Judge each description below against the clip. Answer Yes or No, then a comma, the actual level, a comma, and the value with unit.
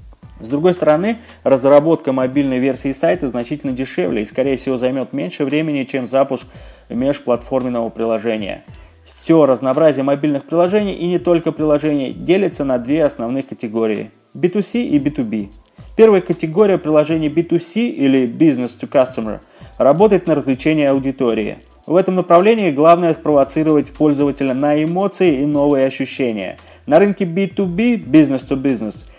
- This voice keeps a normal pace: Yes, average, 130 wpm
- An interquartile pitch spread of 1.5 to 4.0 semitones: No, average, 4.5 semitones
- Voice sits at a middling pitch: Yes, medium, 145 Hz